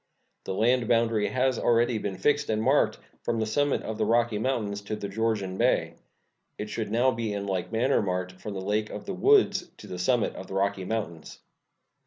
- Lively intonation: No, average, 3.1 semitones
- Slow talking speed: No, fast, 205 wpm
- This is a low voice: Yes, low, 110 Hz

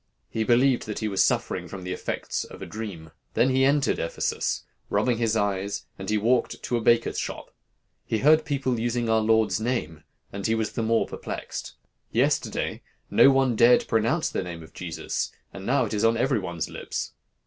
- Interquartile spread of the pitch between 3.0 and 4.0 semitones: Yes, average, 3.5 semitones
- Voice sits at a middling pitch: No, low, 115 Hz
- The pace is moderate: Yes, average, 190 wpm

